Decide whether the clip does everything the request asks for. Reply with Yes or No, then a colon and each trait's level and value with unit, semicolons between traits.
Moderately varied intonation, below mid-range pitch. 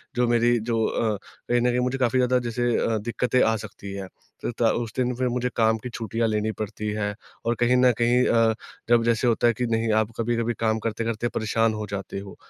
No: narrow, 1.7 semitones; low, 115 Hz